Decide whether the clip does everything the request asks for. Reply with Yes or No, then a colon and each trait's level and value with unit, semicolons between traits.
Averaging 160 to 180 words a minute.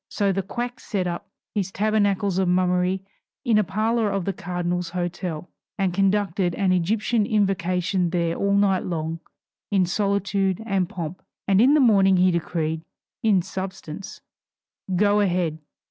No: average, 145 wpm